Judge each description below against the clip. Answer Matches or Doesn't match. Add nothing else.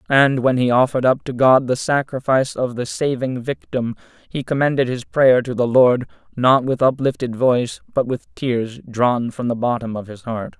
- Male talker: Matches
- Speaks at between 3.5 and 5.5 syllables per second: Matches